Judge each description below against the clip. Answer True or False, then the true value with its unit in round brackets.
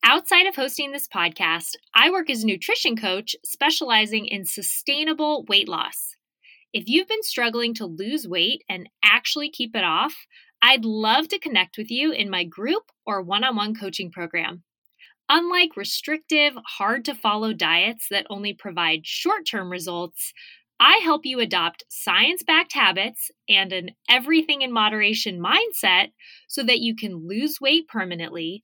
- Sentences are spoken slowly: False (155 wpm)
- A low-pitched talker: False (230 Hz)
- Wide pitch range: True (7.6 semitones)